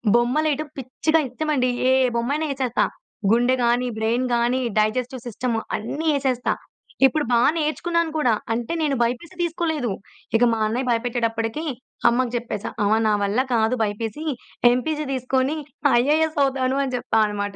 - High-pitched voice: Yes, very high, 250 Hz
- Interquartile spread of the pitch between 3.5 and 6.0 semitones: Yes, average, 4.2 semitones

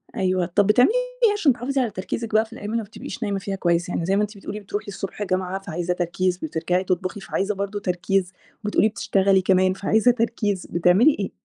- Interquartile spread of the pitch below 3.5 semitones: Yes, narrow, 2.5 semitones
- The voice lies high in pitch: Yes, high, 195 Hz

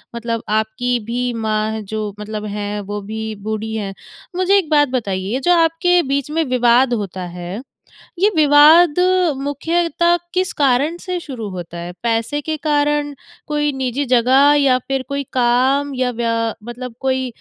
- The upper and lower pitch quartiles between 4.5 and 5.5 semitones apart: Yes, average, 5.2 semitones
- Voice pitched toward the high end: Yes, very high, 255 Hz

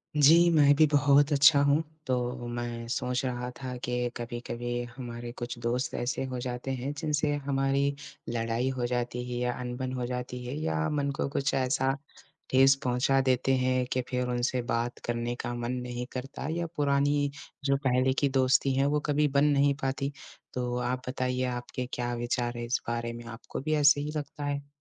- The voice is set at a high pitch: No, low, 125 Hz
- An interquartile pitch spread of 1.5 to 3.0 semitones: Yes, narrow, 2.5 semitones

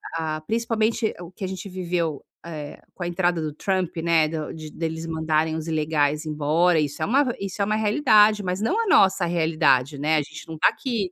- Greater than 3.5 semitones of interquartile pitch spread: Yes, average, 3.9 semitones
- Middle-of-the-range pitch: Yes, medium, 170 Hz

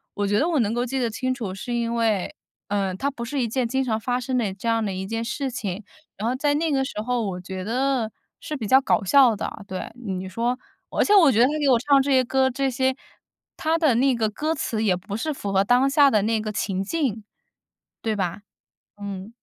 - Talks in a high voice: Yes, high, 235 Hz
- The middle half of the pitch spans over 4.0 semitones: Yes, average, 4.6 semitones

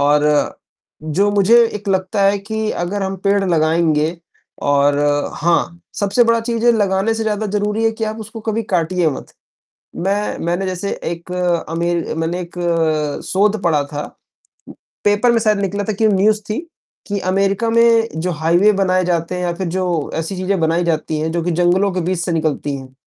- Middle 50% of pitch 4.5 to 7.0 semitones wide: No, average, 3.6 semitones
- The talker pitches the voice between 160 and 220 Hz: Yes, high, 190 Hz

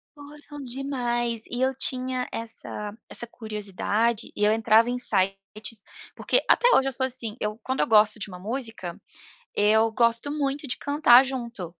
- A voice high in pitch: Yes, high, 235 Hz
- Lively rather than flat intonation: No, average, 3.6 semitones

